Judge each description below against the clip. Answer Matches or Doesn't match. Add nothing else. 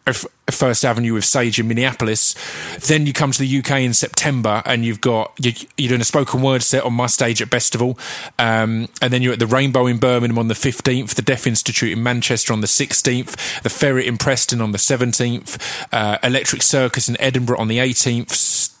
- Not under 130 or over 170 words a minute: Doesn't match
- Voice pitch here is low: Matches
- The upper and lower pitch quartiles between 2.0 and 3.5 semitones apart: Matches